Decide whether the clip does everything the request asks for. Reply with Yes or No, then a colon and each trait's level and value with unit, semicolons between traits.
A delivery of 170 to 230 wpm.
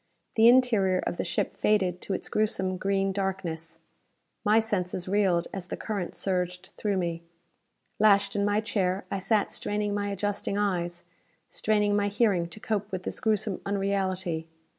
No: average, 160 wpm